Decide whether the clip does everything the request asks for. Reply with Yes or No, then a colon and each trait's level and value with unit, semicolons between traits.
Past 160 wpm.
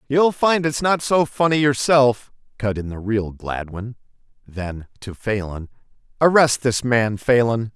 No: average, 145 wpm